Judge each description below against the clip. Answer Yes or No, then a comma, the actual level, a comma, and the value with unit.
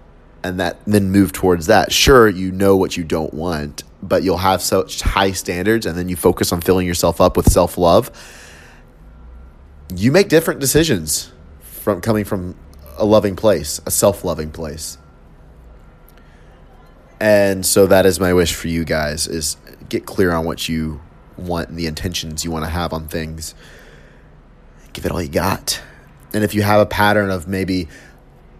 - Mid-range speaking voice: No, very low, 85 Hz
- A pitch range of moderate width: Yes, average, 3.6 semitones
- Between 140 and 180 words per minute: Yes, average, 170 wpm